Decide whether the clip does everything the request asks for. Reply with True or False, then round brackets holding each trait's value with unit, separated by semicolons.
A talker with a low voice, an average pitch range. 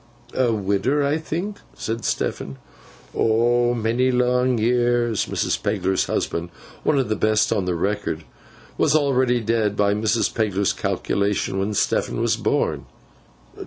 True (115 Hz; 3.5 semitones)